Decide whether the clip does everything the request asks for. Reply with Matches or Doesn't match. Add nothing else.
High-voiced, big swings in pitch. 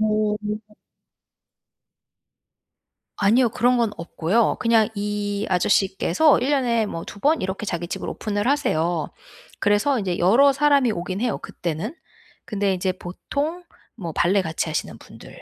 Doesn't match